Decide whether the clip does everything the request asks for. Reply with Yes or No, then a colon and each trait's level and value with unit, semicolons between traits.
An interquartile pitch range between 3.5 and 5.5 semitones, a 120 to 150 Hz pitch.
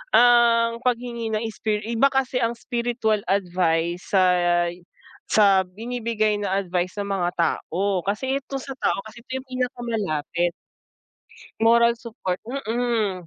No: average, 3.9 semitones; high, 220 Hz